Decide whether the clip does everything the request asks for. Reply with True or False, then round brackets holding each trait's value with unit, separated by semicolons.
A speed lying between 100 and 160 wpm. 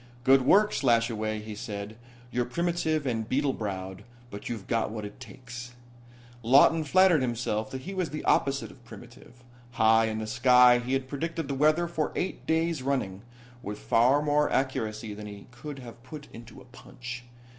False (175 wpm)